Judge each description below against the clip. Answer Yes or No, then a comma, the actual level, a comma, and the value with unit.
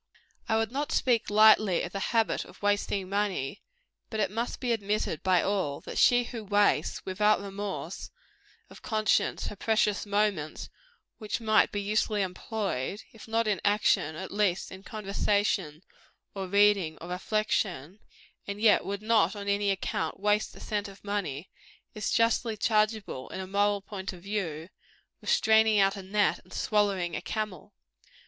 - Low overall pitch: No, high, 205 Hz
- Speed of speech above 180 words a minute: No, average, 160 wpm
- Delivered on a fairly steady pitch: Yes, narrow, 2.0 semitones